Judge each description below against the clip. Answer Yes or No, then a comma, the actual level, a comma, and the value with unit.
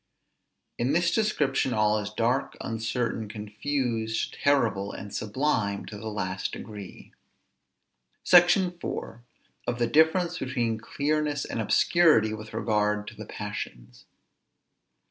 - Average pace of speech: No, slow, 115 wpm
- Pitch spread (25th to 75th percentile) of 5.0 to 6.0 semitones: Yes, average, 5.3 semitones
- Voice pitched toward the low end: Yes, low, 115 Hz